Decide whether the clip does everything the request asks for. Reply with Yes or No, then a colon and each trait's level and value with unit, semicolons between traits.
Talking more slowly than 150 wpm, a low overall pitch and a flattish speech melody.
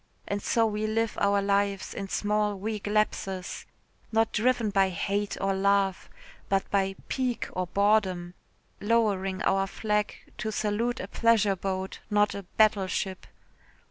No: average, 140 wpm; high, 200 Hz; narrow, 1.8 semitones